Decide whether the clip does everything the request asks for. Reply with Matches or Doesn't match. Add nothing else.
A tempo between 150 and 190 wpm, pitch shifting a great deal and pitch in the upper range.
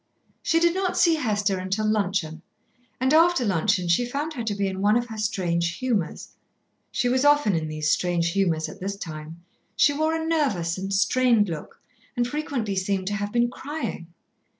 Matches